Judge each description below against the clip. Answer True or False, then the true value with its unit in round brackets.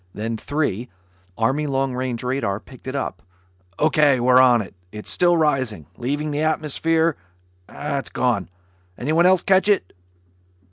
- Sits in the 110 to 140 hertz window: True (135 Hz)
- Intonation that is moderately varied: True (4.2 semitones)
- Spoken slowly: True (130 wpm)